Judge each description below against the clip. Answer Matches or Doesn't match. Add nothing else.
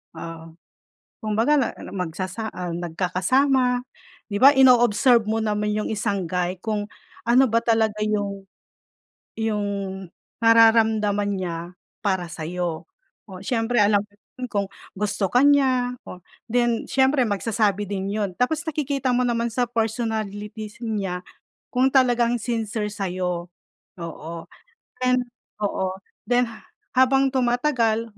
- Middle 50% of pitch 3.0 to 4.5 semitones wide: Matches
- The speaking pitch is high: Matches